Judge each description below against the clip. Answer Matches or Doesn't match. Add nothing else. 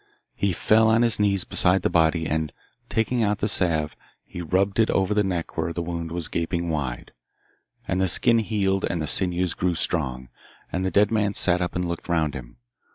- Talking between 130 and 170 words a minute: Doesn't match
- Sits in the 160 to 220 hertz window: Doesn't match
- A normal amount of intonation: Matches